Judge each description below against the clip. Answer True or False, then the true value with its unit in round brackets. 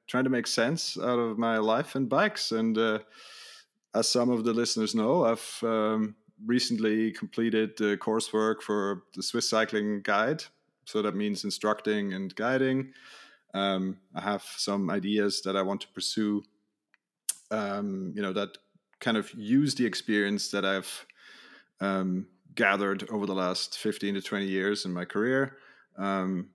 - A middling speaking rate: True (155 wpm)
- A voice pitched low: True (105 Hz)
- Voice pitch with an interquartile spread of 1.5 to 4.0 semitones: True (2.7 semitones)